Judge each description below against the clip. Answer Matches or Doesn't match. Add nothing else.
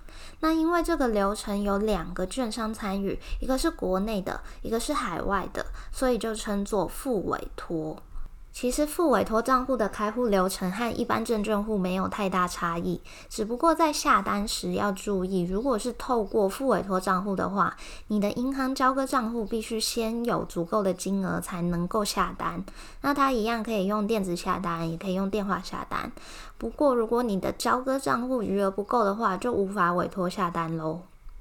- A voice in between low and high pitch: Doesn't match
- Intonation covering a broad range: Doesn't match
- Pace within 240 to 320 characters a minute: Matches